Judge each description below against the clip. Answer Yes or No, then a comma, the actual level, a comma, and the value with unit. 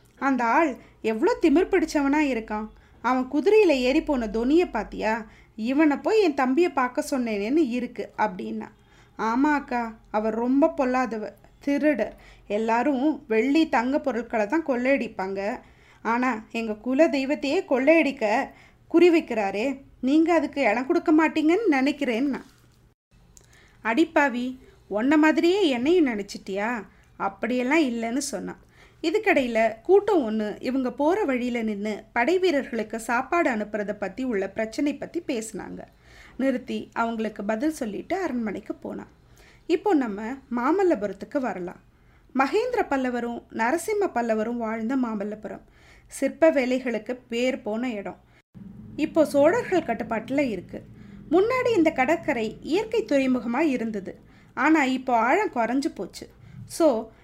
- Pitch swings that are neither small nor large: No, wide, 5.8 semitones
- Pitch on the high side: Yes, very high, 260 Hz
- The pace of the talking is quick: No, average, 110 wpm